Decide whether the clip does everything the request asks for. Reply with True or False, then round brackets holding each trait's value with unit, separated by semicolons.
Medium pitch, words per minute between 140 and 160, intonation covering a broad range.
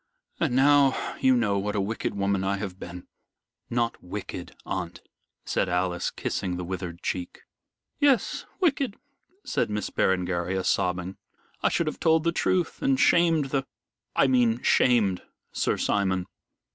False (105 Hz; 145 wpm; 7.4 semitones)